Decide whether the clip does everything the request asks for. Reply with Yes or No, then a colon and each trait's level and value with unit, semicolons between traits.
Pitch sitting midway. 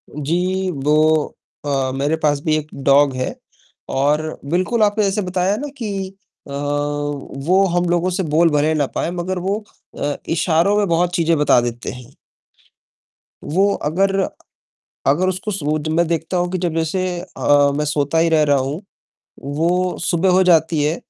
Yes: medium, 165 Hz